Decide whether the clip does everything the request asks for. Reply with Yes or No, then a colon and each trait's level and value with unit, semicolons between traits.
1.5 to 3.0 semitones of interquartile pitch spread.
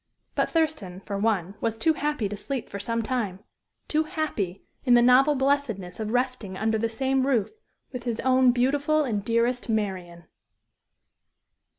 No: average, 4.6 semitones